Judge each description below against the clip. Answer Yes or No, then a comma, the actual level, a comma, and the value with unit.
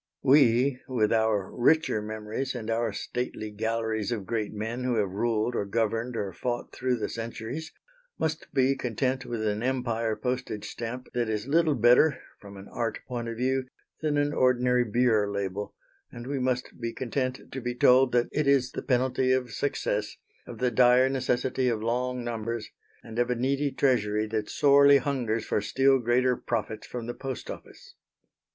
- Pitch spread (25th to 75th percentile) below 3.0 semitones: Yes, narrow, 2.6 semitones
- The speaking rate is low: No, average, 175 wpm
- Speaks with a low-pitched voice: Yes, low, 120 Hz